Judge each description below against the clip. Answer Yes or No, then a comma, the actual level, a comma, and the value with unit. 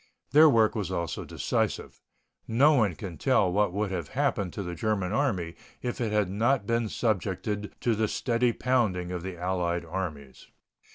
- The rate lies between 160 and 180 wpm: Yes, average, 170 wpm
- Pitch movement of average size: Yes, average, 4.5 semitones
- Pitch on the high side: No, low, 105 Hz